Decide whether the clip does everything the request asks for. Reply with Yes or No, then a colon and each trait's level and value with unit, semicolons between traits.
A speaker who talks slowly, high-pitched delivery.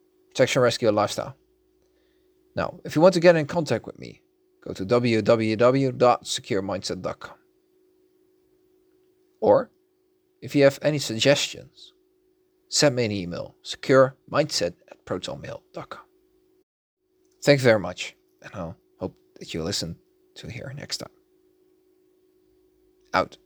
Yes: slow, 115 wpm; very high, 360 Hz